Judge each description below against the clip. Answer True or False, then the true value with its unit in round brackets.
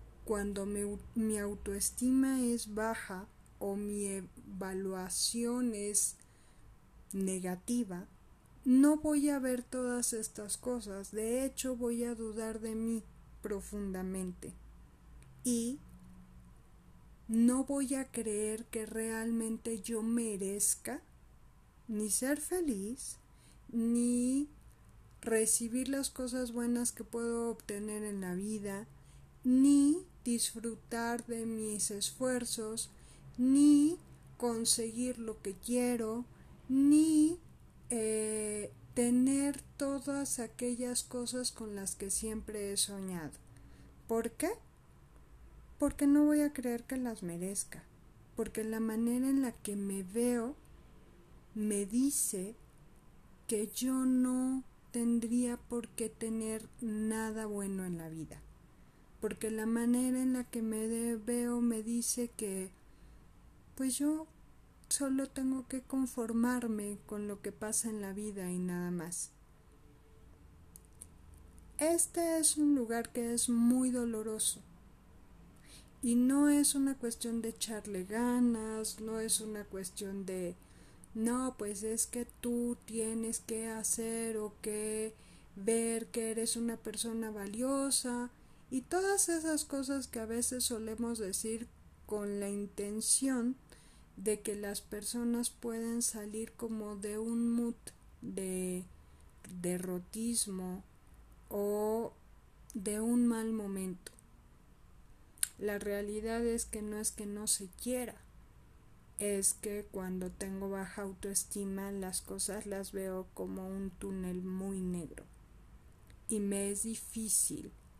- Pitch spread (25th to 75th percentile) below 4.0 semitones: True (3.3 semitones)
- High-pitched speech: True (225 Hz)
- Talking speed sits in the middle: False (115 wpm)